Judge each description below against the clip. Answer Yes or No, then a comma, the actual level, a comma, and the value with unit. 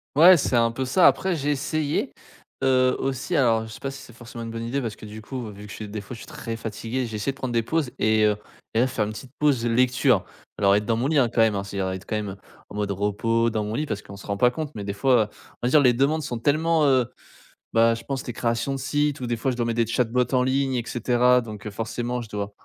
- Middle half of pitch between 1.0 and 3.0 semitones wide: No, average, 3.4 semitones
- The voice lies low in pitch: Yes, low, 120 Hz